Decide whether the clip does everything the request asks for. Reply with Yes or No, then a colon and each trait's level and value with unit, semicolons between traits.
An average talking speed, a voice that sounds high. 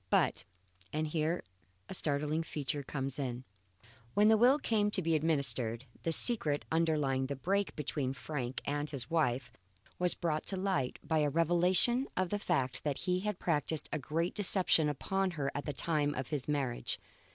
No: average, 175 wpm; medium, 155 Hz